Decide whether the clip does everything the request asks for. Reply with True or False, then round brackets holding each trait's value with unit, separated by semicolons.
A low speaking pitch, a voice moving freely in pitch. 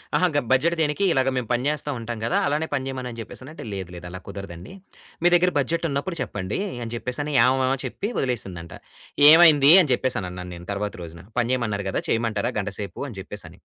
True (120 Hz; 6.2 semitones)